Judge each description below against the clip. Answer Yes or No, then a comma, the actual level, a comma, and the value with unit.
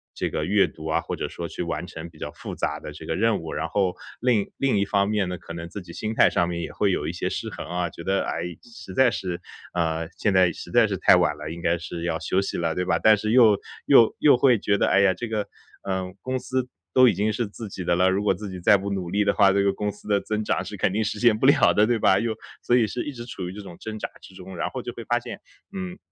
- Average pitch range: Yes, average, 3.7 semitones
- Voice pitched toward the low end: Yes, low, 100 Hz